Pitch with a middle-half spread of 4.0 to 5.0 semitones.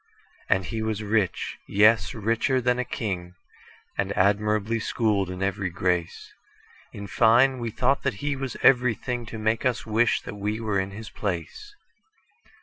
No: average, 3.3 semitones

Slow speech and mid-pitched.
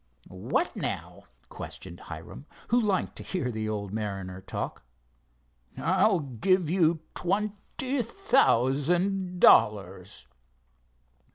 Yes: slow, 100 wpm; medium, 155 Hz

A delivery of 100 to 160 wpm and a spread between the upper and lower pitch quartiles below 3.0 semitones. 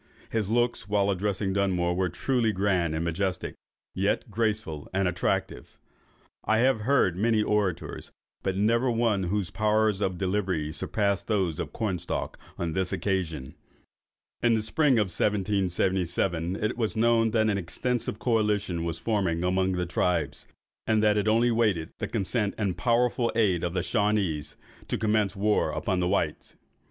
No: average, 155 wpm; average, 3.4 semitones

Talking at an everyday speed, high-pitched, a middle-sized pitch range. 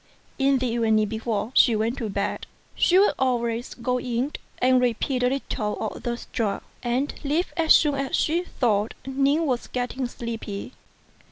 Yes: average, 165 wpm; high, 245 Hz; average, 3.2 semitones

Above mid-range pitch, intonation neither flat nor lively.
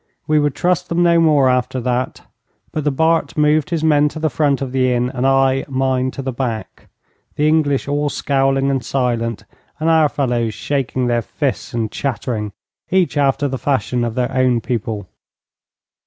No: low, 135 Hz; average, 3.1 semitones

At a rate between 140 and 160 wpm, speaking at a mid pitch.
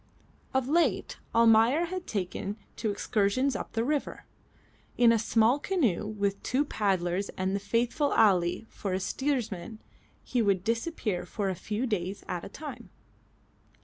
No: average, 145 wpm; high, 220 Hz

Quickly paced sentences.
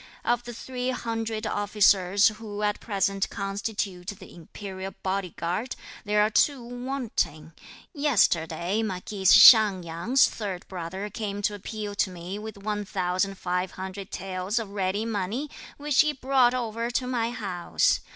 No: average, 145 wpm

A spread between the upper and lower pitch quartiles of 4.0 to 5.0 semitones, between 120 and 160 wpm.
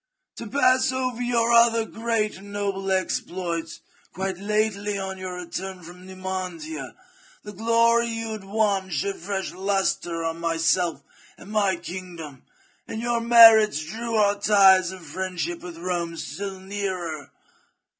No: average, 3.5 semitones; slow, 135 wpm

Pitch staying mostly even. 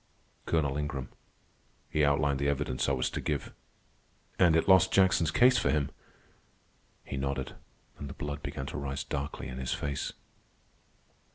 Yes: narrow, 2.3 semitones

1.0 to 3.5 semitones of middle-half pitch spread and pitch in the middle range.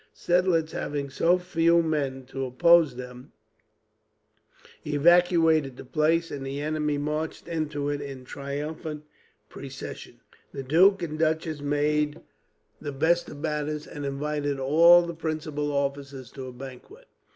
Yes: average, 2.7 semitones; medium, 150 Hz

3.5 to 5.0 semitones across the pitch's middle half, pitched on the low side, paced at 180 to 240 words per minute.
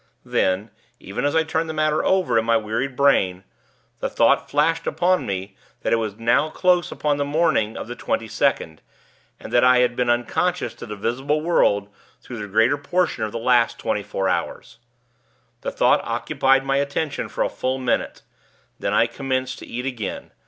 Yes: average, 4.7 semitones; low, 125 Hz; average, 190 wpm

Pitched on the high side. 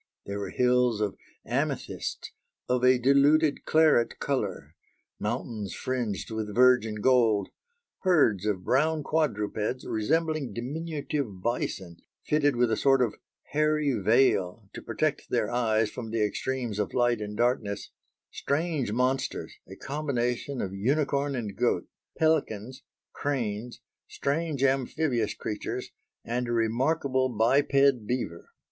No: low, 125 Hz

